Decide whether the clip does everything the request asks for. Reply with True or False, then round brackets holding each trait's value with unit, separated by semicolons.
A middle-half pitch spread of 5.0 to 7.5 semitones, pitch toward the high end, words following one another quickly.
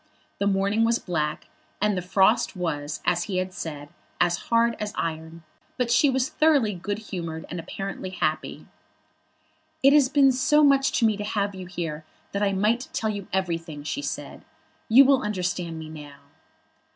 False (5.5 semitones; 195 Hz; 175 wpm)